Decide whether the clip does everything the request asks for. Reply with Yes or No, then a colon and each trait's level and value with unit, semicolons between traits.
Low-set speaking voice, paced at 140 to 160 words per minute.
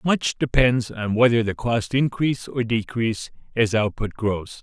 Yes: low, 115 Hz; average, 155 wpm